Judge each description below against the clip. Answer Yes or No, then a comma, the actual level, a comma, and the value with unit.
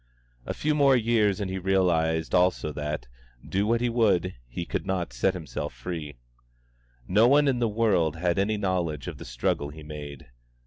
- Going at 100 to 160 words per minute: No, average, 180 wpm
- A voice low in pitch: Yes, very low, 90 Hz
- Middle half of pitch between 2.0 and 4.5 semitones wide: No, wide, 5.6 semitones